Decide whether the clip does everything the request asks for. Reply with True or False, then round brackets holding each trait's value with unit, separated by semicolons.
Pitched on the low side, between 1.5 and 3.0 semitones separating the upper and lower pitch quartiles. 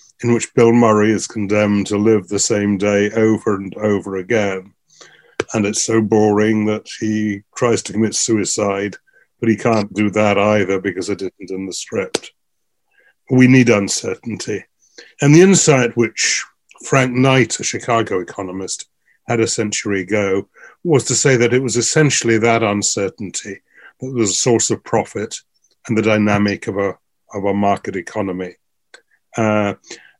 True (105 Hz; 2.6 semitones)